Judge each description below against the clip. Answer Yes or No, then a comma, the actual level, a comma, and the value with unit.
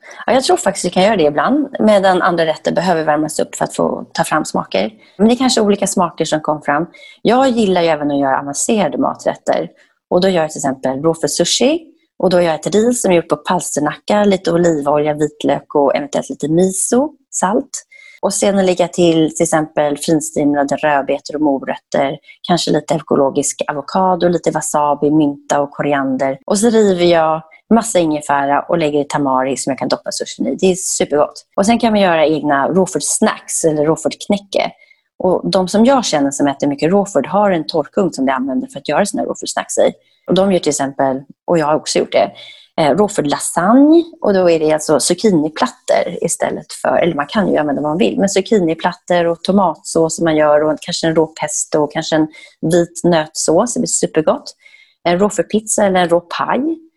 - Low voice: No, medium, 170 Hz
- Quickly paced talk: Yes, fast, 200 wpm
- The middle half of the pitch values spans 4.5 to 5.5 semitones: Yes, average, 5.0 semitones